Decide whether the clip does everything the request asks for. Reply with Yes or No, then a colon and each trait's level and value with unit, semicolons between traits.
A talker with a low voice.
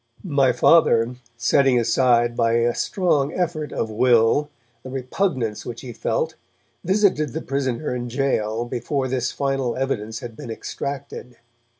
Yes: low, 125 Hz